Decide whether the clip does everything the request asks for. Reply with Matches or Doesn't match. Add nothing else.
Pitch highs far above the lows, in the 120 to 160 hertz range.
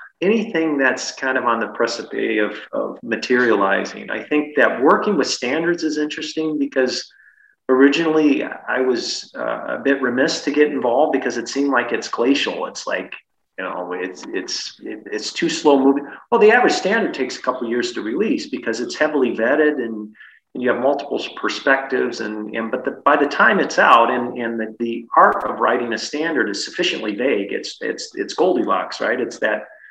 Doesn't match